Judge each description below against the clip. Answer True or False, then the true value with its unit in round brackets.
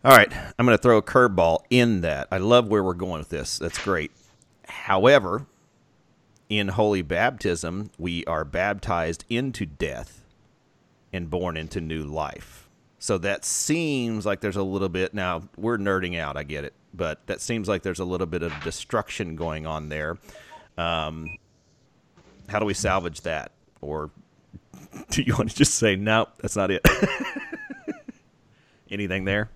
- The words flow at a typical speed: True (165 wpm)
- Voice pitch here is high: False (95 Hz)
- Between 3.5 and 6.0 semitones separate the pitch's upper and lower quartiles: True (4.5 semitones)